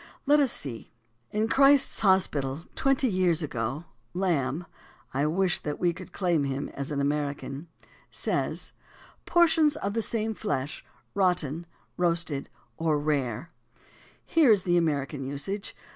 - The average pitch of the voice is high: No, medium, 170 Hz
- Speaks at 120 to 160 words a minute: Yes, average, 140 wpm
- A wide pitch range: Yes, wide, 6.1 semitones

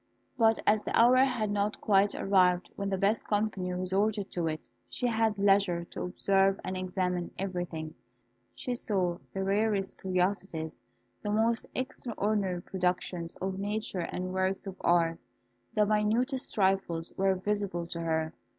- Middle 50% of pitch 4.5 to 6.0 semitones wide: No, average, 2.7 semitones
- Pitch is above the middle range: Yes, high, 195 Hz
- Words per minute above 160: No, average, 145 wpm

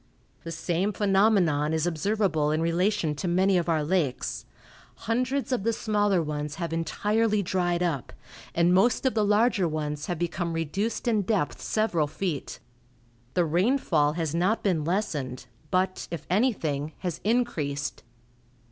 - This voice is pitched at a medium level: Yes, medium, 175 Hz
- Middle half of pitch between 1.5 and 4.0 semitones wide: No, average, 4.9 semitones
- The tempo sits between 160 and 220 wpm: No, average, 145 wpm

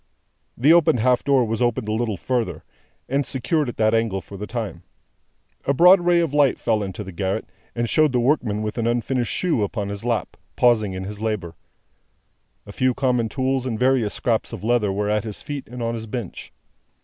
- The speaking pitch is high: No, low, 115 Hz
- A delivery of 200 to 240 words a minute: Yes, fast, 205 wpm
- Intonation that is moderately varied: Yes, average, 3.6 semitones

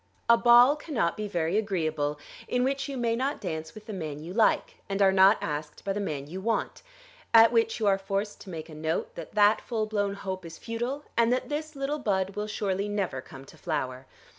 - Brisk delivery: Yes, fast, 220 wpm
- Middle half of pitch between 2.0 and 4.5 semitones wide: No, wide, 5.5 semitones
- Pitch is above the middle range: Yes, high, 200 Hz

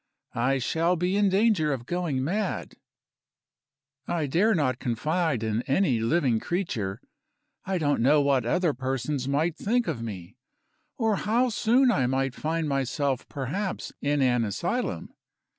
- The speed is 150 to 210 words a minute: No, average, 140 wpm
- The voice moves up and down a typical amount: No, wide, 6.0 semitones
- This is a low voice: No, medium, 145 Hz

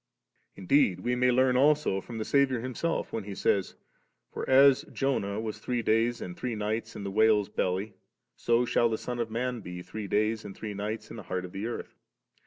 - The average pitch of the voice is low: Yes, low, 110 Hz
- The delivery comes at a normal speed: No, fast, 215 wpm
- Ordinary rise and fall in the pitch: Yes, average, 3.5 semitones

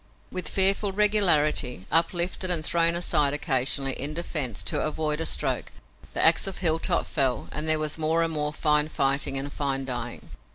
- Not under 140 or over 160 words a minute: No, average, 170 wpm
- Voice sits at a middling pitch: Yes, medium, 155 Hz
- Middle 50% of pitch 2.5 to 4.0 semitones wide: Yes, average, 3.5 semitones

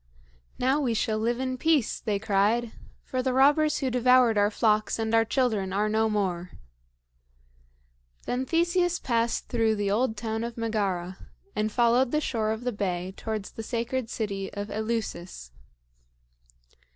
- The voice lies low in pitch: No, high, 225 Hz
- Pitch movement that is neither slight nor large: Yes, average, 3.3 semitones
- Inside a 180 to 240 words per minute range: No, average, 150 wpm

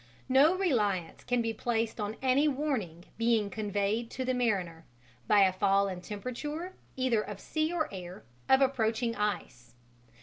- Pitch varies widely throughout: No, average, 4.6 semitones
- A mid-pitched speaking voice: No, high, 225 Hz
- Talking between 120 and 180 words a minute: Yes, average, 155 wpm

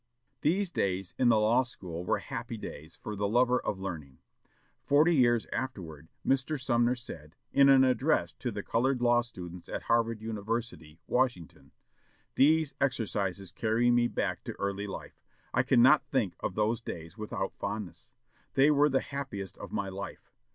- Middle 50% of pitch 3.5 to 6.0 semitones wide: Yes, average, 5.1 semitones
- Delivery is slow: No, average, 160 wpm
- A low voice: Yes, low, 115 Hz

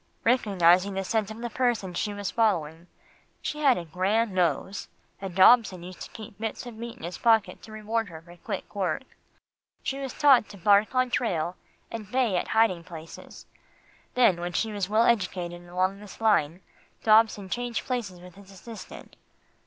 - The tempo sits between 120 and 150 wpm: No, average, 175 wpm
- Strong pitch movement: No, average, 4.0 semitones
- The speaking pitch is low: No, high, 205 Hz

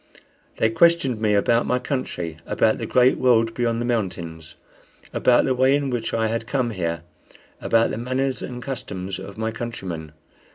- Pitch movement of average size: Yes, average, 4.0 semitones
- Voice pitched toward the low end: Yes, low, 115 Hz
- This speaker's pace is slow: No, average, 170 wpm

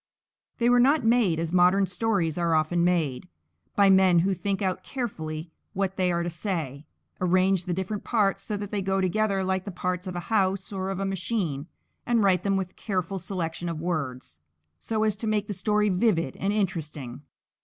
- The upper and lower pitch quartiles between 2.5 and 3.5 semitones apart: Yes, average, 2.9 semitones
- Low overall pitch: No, high, 190 Hz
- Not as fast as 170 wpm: No, average, 195 wpm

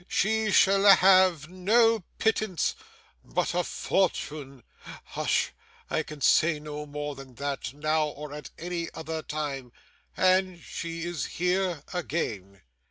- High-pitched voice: No, medium, 165 Hz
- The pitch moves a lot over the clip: No, average, 4.0 semitones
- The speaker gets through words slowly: Yes, slow, 125 wpm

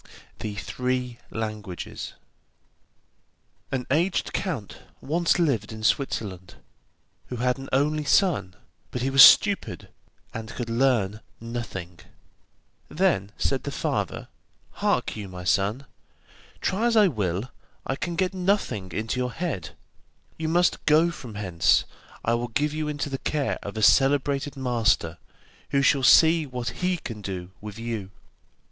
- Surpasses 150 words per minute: No, average, 140 wpm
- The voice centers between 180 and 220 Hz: No, low, 125 Hz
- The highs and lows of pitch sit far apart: Yes, wide, 6.2 semitones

